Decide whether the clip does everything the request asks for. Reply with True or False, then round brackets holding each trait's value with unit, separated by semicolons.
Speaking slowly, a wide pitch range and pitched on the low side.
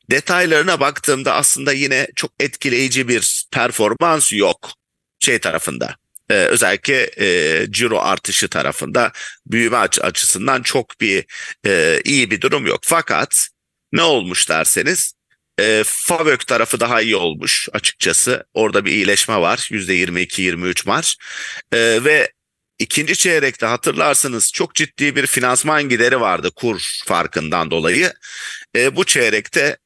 True (120 wpm; 7.9 semitones; 130 Hz)